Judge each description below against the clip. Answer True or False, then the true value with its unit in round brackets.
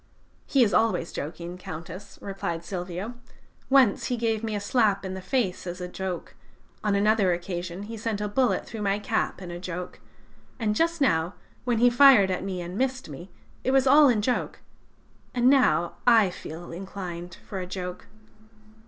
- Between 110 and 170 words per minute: False (180 wpm)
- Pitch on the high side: True (200 Hz)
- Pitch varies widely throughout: False (4.4 semitones)